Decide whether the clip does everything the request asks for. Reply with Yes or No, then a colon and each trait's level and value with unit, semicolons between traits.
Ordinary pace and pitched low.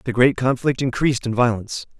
Yes: average, 180 wpm; low, 125 Hz